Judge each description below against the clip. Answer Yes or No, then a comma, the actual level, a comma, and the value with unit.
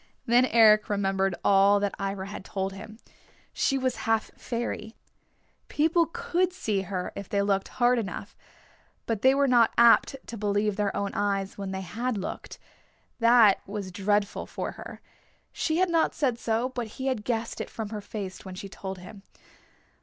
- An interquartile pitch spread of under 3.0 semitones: No, average, 3.5 semitones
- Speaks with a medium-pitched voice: No, high, 210 Hz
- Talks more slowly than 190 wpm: Yes, average, 175 wpm